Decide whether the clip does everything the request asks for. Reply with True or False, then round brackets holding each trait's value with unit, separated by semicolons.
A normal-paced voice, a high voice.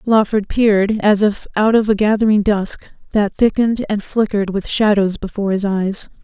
True (175 wpm; 205 Hz)